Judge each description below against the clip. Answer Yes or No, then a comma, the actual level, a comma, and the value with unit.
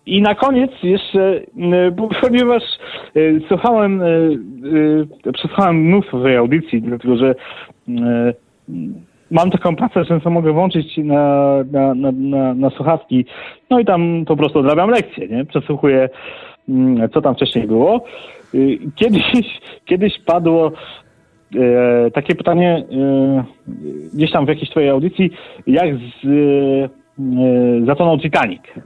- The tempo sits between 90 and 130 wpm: Yes, slow, 110 wpm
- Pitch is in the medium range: Yes, medium, 155 Hz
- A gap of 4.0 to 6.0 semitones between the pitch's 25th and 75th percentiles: Yes, average, 5.2 semitones